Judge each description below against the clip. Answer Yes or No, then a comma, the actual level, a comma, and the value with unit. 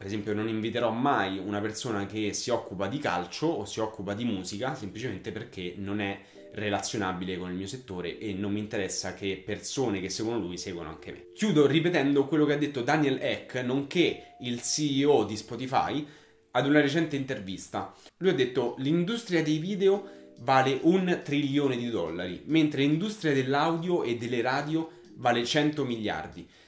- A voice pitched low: Yes, low, 130 Hz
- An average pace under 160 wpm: No, fast, 170 wpm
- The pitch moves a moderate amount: No, wide, 6.3 semitones